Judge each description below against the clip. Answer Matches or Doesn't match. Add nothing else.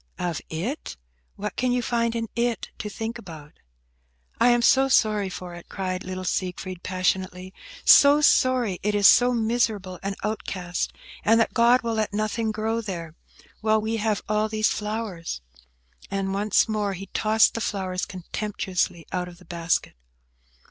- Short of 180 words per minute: Matches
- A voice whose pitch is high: Matches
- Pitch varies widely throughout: Doesn't match